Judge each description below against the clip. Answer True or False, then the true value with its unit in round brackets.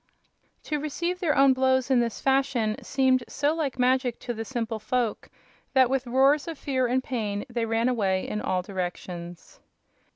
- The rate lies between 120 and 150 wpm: False (170 wpm)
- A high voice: True (255 Hz)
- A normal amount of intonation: True (3.2 semitones)